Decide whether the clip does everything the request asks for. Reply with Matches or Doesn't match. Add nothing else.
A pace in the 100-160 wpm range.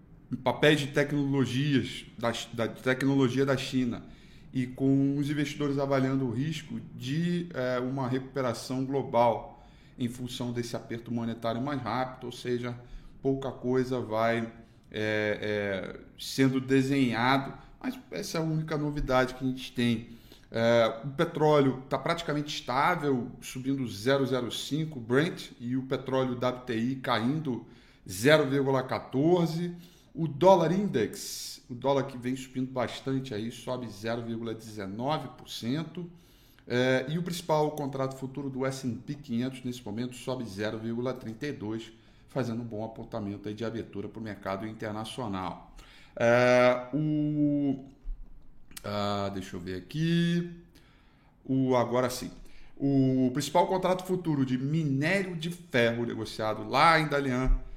Matches